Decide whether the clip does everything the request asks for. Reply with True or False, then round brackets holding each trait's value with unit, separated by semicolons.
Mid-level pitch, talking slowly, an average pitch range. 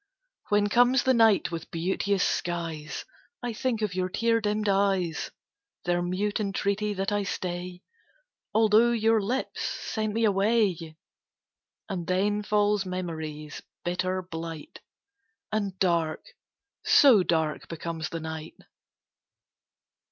False (195 Hz; 115 wpm; 3.6 semitones)